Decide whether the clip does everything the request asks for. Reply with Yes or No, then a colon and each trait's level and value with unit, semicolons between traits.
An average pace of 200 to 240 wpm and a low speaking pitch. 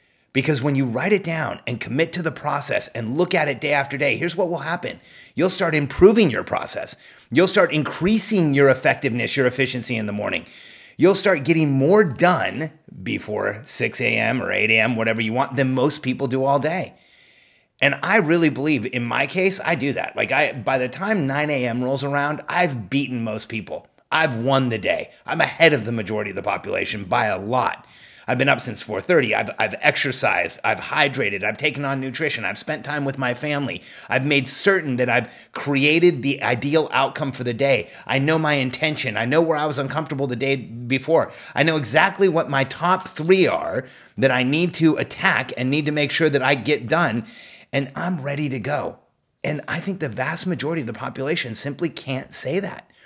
No: fast, 205 wpm; medium, 145 Hz